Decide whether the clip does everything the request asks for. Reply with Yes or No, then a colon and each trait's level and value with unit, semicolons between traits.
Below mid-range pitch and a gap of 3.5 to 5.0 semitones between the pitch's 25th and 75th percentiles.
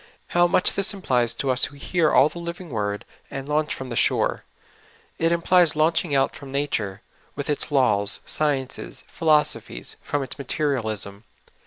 No: medium, 145 Hz; average, 4.6 semitones